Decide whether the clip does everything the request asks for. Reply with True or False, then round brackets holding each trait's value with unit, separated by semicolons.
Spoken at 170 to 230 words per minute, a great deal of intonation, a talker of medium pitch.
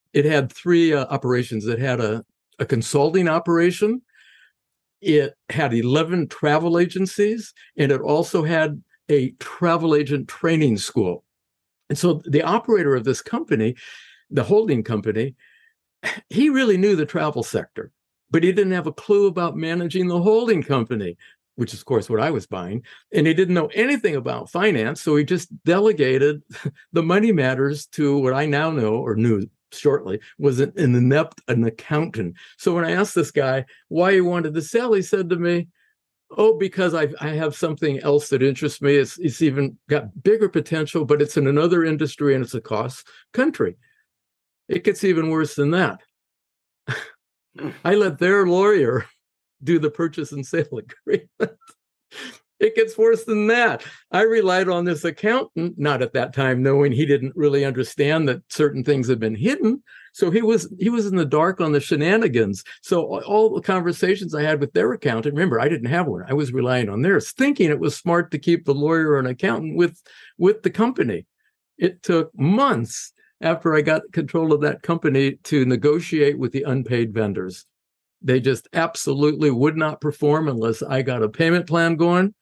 False (180 wpm; 4.4 semitones; 155 Hz)